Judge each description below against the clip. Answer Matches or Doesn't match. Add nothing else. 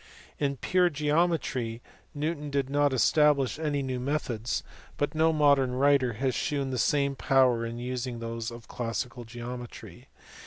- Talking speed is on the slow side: Doesn't match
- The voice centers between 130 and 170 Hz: Matches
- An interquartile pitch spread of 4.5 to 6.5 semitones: Doesn't match